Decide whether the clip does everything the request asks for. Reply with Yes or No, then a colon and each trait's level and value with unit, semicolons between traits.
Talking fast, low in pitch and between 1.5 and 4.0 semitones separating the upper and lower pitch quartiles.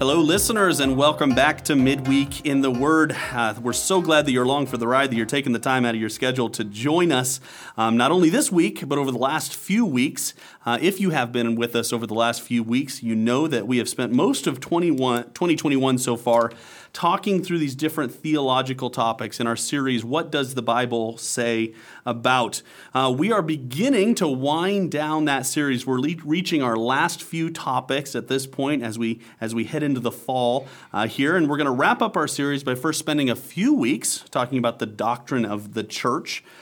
No: fast, 215 wpm; low, 130 Hz; average, 4.4 semitones